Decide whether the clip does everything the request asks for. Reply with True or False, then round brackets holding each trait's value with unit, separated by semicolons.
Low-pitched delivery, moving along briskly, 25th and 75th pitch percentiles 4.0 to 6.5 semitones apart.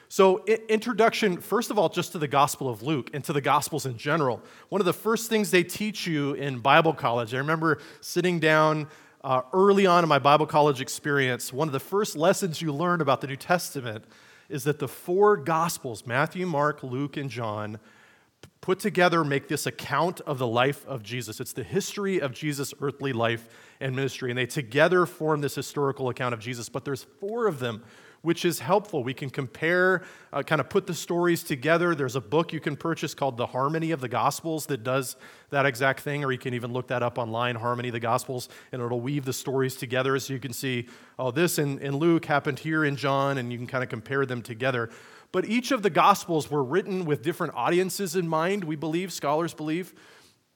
False (145 Hz; 210 wpm; 4.6 semitones)